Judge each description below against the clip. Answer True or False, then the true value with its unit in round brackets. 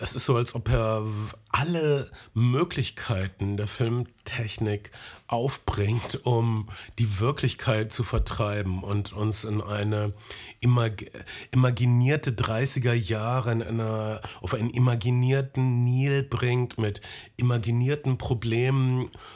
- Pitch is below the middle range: True (120 Hz)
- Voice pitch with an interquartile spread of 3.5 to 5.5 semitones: False (2.8 semitones)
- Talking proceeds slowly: True (105 wpm)